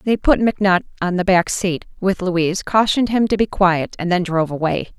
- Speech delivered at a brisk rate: Yes, fast, 215 wpm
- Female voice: Yes, female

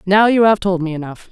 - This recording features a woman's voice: Yes, female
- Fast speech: Yes, fast, 275 wpm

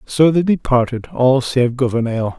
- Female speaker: No, male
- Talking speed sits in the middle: Yes, average, 150 wpm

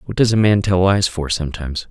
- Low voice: Yes, very low, 95 Hz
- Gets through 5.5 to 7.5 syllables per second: Yes, 5.9 syllables/s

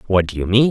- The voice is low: Yes, low, 105 Hz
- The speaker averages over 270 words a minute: Yes, fast, 340 wpm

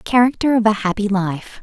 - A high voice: Yes, high, 215 Hz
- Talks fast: No, average, 185 wpm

